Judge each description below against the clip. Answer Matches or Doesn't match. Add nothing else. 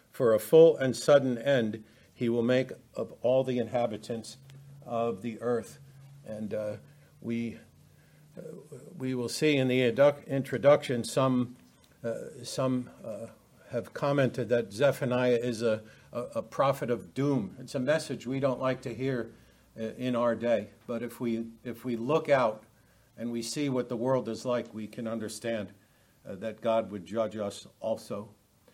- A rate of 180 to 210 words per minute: Doesn't match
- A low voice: Matches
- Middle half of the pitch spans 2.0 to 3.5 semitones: Matches